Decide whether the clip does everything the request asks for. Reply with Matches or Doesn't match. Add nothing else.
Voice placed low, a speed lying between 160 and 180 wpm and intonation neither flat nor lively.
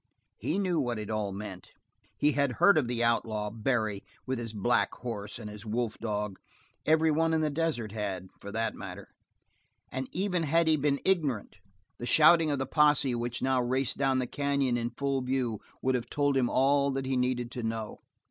Doesn't match